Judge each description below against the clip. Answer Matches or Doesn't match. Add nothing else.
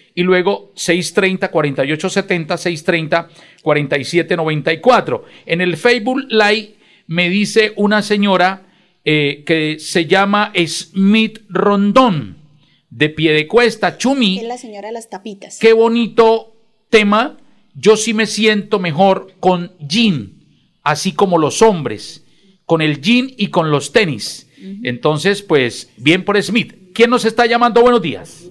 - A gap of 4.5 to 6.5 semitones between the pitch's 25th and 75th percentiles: Matches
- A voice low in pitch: Doesn't match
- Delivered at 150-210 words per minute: Doesn't match